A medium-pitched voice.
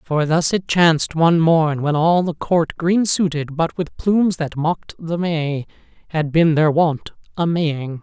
Yes: medium, 160 Hz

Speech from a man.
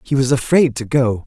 Yes: male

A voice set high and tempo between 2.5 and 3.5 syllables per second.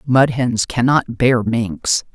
No: low, 120 Hz; 3.1 syllables/s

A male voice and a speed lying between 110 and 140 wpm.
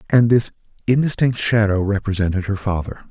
Yes: male; slow, 135 wpm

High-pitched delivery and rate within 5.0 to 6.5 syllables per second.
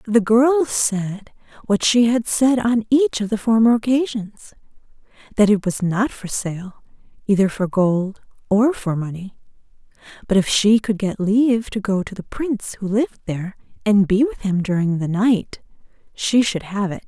No: high, 215 Hz; 4.6 syllables/s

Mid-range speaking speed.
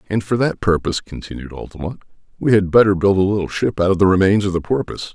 No: fast, 235 wpm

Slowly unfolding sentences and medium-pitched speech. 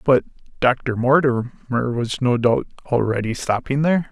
No: slow, 130 wpm; low, 125 Hz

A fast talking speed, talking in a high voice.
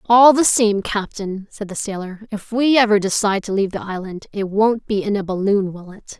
Yes: fast, 225 wpm; high, 205 Hz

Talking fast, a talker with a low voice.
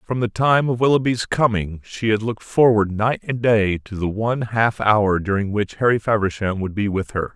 Yes: fast, 210 wpm; low, 110 Hz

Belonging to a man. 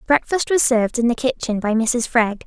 No: female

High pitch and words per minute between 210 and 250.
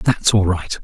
No: low, 100 Hz; fast, 215 wpm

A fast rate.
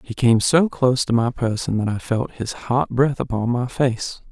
Yes: fast, 225 wpm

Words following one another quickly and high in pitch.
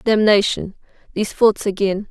No: slow, 115 wpm; high, 205 Hz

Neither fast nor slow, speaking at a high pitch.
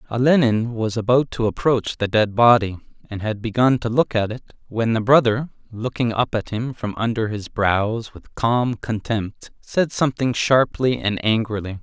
No: average, 175 wpm; low, 115 Hz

